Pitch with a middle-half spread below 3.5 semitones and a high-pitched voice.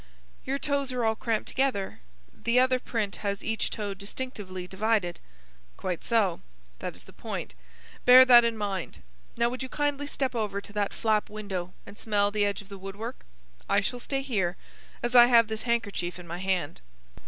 No: average, 3.8 semitones; high, 215 Hz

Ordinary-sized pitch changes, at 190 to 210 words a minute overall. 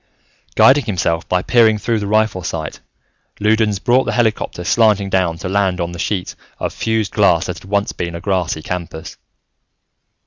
No: average, 3.8 semitones; average, 170 wpm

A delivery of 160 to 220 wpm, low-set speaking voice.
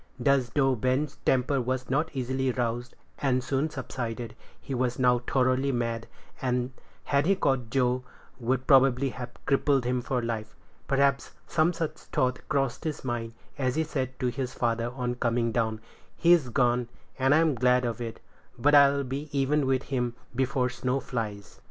Yes: average, 165 wpm; low, 130 Hz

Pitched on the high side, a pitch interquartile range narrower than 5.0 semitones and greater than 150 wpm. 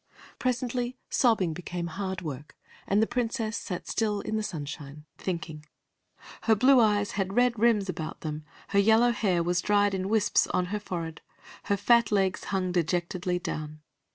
Yes: high, 195 Hz; average, 4.3 semitones; average, 160 wpm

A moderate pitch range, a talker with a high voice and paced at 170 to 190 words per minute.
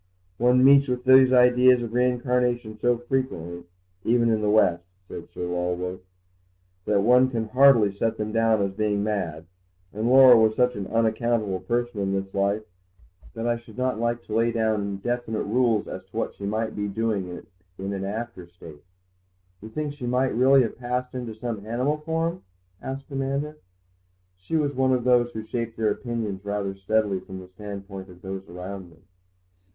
No: average, 3.8 semitones; low, 115 Hz; average, 180 wpm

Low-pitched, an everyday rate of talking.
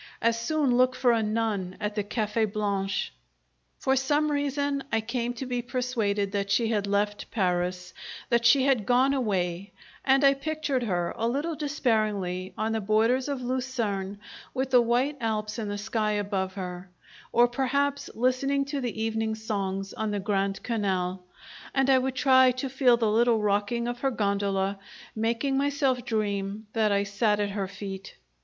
No: high, 225 Hz; average, 170 wpm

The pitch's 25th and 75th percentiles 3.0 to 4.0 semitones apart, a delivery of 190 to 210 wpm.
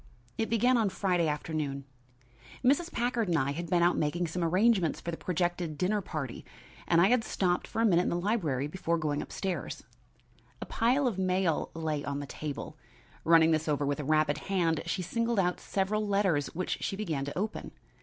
No: average, 4.5 semitones; average, 195 wpm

